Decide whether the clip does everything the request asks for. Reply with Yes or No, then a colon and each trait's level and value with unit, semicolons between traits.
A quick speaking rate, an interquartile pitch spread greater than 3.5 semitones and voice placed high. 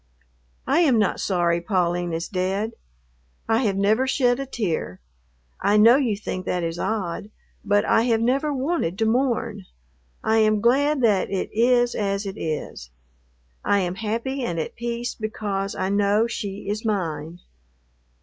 No: average, 160 wpm; average, 4.0 semitones; high, 210 Hz